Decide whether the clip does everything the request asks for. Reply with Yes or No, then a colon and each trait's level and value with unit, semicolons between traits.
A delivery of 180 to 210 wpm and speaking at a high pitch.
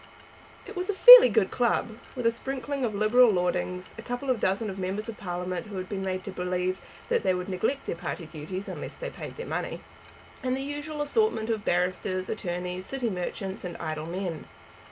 Yes: average, 200 wpm; high, 195 Hz